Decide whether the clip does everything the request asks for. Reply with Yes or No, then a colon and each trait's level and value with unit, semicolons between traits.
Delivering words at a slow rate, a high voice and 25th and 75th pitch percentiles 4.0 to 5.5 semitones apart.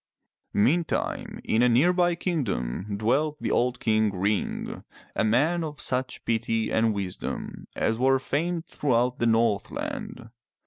No: slow, 130 wpm; low, 120 Hz; average, 5.2 semitones